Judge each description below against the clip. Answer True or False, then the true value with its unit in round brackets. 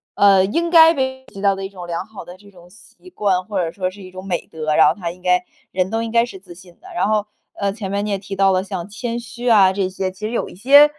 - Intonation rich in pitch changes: False (3.4 semitones)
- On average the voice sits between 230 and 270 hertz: False (195 Hz)